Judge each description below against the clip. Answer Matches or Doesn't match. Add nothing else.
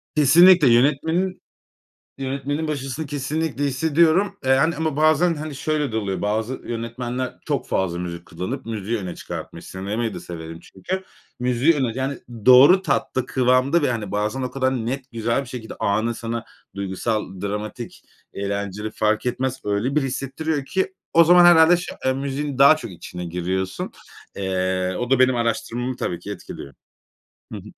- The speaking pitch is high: Doesn't match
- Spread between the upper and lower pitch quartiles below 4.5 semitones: Doesn't match